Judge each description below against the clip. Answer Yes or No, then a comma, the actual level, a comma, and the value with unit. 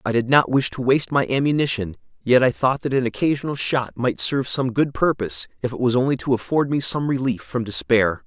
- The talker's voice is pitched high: No, low, 130 Hz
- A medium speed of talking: No, fast, 225 wpm